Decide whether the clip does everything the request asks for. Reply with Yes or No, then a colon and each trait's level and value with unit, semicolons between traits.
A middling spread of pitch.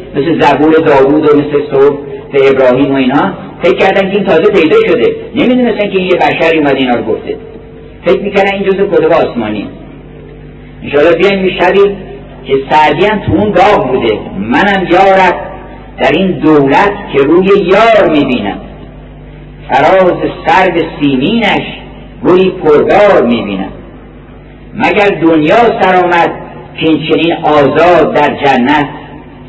Yes: average, 5.0 semitones